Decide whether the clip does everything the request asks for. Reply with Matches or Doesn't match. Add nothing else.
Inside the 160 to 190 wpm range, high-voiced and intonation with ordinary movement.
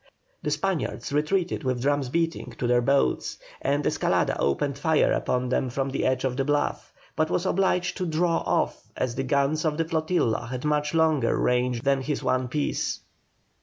Doesn't match